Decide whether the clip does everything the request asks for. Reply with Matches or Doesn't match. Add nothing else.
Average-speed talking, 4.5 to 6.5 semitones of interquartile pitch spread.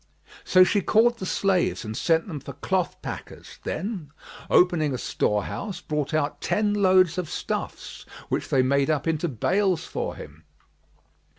Matches